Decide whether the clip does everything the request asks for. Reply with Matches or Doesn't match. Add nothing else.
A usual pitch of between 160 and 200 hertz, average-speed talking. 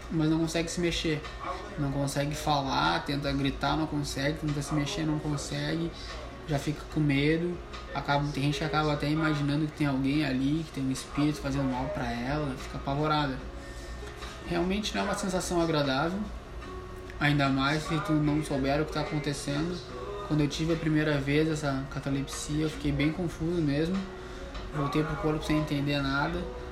Doesn't match